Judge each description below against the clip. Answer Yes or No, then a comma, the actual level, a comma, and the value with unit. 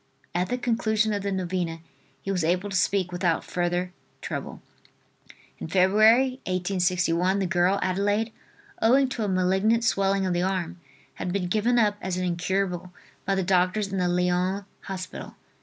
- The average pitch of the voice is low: No, high, 190 Hz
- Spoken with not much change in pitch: Yes, narrow, 2.3 semitones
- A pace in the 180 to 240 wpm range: No, average, 155 wpm